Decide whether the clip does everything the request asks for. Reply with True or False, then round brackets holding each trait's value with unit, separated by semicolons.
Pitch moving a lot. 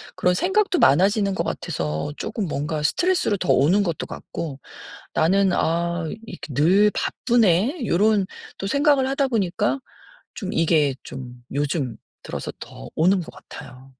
True (6.3 semitones)